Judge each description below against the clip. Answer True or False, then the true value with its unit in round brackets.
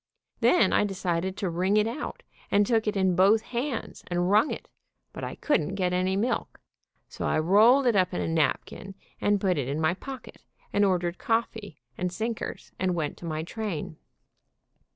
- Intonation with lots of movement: False (3.8 semitones)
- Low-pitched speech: False (190 Hz)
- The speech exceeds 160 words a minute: True (190 wpm)